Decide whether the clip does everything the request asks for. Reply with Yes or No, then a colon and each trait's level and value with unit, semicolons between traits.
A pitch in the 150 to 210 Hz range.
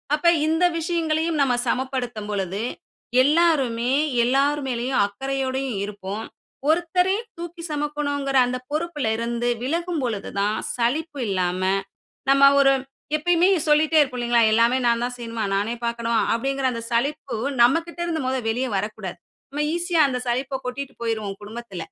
No: very high, 260 Hz